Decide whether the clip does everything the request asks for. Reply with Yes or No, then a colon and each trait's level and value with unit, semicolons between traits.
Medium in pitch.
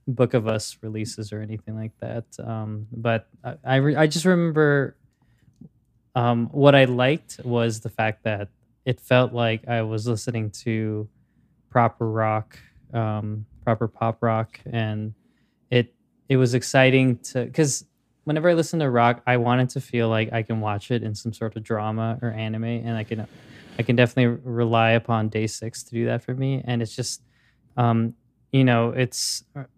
No: low, 120 Hz